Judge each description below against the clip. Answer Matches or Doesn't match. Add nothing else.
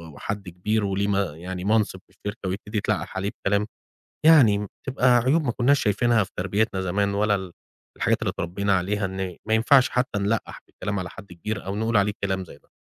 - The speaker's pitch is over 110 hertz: Doesn't match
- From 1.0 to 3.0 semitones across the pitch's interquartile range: Matches